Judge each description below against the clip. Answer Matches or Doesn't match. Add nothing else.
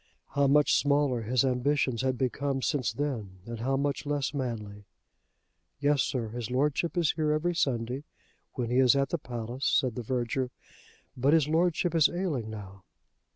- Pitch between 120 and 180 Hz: Matches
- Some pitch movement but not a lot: Matches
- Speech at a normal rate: Matches